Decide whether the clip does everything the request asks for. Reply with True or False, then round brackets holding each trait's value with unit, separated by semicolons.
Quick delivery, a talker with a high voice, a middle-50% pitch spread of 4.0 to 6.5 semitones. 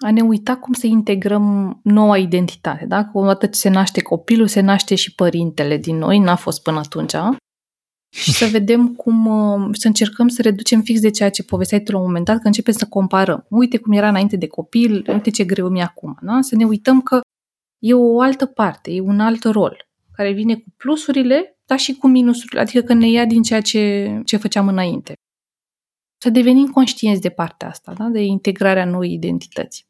False (205 wpm; 215 Hz; 3.2 semitones)